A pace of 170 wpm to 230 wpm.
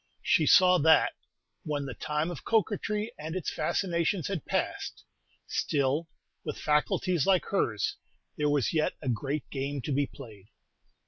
No: average, 145 wpm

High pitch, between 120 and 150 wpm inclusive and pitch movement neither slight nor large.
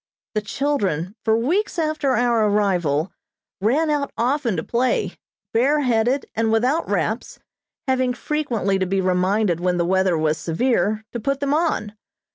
No: high, 225 Hz; average, 145 wpm; wide, 6.4 semitones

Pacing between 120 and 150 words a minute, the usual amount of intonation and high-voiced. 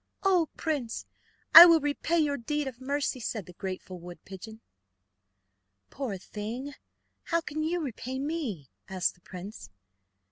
No: average, 140 wpm; wide, 7.6 semitones; very high, 260 Hz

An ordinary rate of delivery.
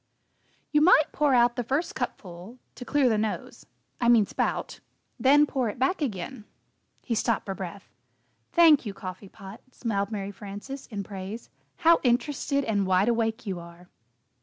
Yes: average, 160 wpm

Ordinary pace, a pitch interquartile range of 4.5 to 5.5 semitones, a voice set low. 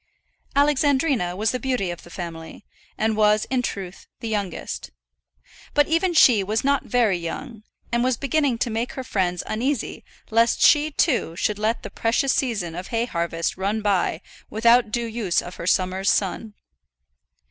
No: average, 165 wpm; average, 5.1 semitones; high, 220 Hz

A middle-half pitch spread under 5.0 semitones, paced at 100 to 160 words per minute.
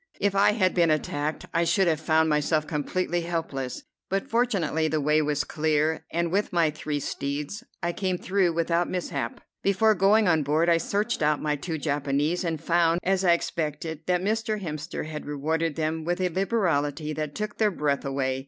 No: average, 3.5 semitones; average, 185 wpm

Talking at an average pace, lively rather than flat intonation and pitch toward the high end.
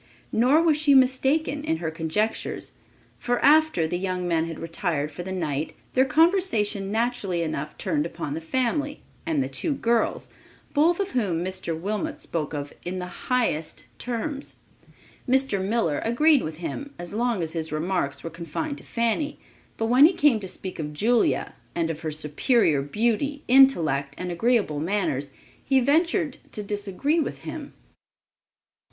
Yes: average, 160 wpm; wide, 8.6 semitones; high, 210 Hz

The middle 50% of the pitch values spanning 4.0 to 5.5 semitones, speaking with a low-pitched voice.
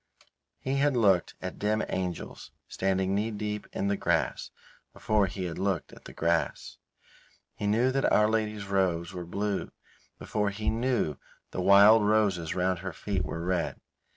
No: average, 2.8 semitones; low, 100 Hz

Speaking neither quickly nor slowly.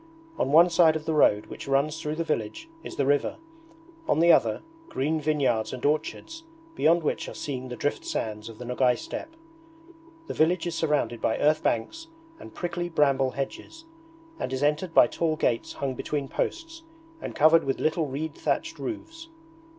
Yes: average, 175 wpm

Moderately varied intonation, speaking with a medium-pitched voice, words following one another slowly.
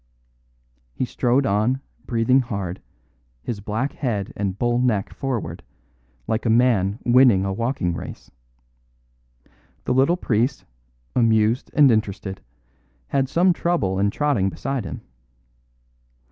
No: average, 4.4 semitones; low, 115 Hz; slow, 120 wpm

